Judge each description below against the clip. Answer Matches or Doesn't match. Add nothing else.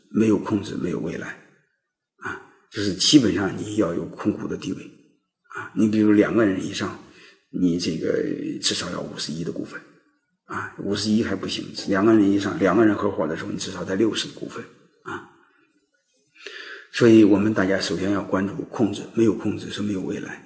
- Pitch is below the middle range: Matches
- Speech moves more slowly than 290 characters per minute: Matches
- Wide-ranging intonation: Doesn't match